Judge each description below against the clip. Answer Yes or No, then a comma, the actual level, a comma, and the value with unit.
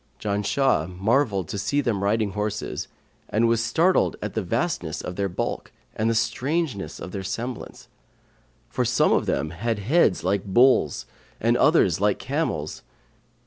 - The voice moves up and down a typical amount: Yes, average, 4.0 semitones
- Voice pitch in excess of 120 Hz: No, low, 105 Hz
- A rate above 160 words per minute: No, average, 150 wpm